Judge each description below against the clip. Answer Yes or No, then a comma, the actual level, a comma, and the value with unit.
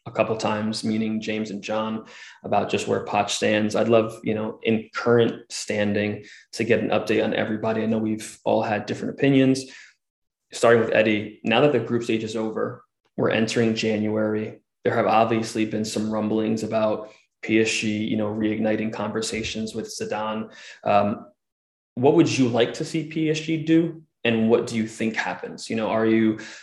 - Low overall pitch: Yes, low, 110 Hz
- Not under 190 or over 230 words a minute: No, average, 180 wpm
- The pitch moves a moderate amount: No, narrow, 1.0 semitones